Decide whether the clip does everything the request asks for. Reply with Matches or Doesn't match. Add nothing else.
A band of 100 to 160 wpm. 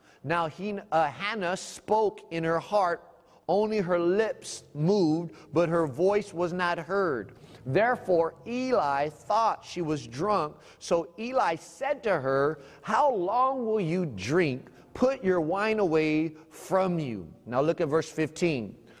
Matches